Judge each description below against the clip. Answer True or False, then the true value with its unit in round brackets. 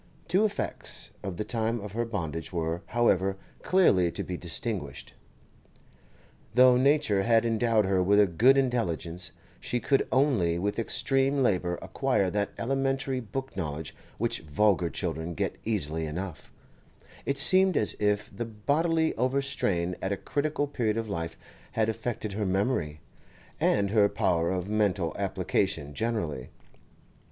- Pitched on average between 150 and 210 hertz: False (105 Hz)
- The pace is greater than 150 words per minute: False (140 wpm)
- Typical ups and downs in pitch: False (5.9 semitones)